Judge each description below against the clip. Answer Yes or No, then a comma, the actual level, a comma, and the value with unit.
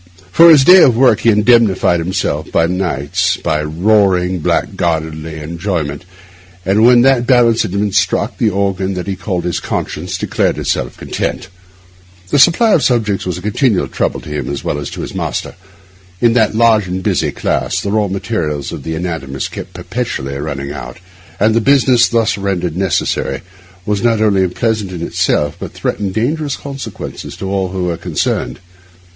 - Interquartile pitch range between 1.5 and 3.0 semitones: No, average, 5.0 semitones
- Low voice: Yes, very low, 95 Hz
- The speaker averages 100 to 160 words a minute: No, average, 175 wpm